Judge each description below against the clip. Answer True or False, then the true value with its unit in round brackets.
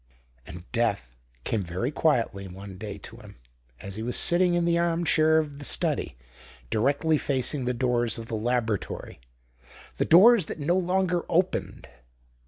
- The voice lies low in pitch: True (130 Hz)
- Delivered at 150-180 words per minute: True (160 wpm)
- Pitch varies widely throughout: True (7.4 semitones)